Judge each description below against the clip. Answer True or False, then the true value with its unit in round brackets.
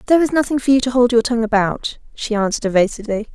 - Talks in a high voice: True (235 Hz)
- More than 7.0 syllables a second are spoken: True (7.7 syllables/s)